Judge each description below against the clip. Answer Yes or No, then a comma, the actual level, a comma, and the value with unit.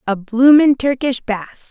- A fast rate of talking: No, average, 140 wpm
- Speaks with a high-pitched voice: Yes, very high, 250 Hz